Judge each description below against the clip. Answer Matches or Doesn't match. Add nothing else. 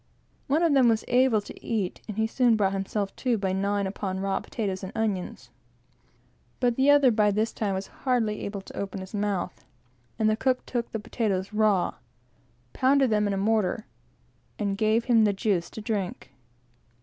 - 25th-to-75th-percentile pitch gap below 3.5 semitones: Matches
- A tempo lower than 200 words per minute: Matches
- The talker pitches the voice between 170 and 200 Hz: Doesn't match